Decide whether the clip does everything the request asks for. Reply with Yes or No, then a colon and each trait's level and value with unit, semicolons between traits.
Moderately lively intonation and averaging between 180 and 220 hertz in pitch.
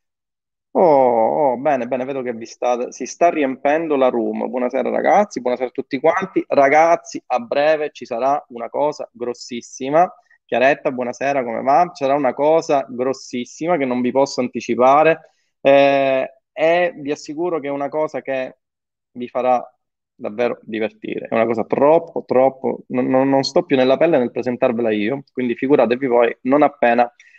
No: average, 3.5 semitones; low, 135 Hz